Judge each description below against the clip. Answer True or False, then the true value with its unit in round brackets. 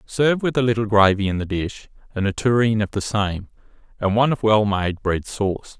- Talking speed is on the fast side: True (220 wpm)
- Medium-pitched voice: False (105 Hz)